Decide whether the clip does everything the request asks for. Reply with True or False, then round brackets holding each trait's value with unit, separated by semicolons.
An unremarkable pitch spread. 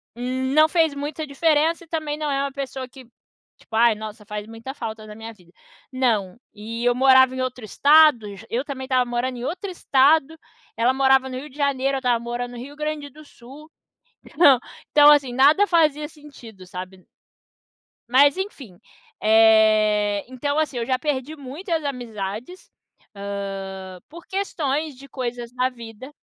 True (4.5 semitones)